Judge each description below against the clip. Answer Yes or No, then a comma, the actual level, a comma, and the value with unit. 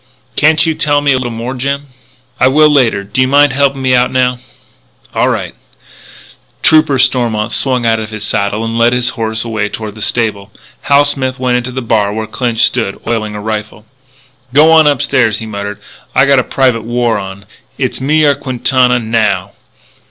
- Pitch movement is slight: No, average, 3.5 semitones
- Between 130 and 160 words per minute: No, average, 185 wpm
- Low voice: Yes, low, 125 Hz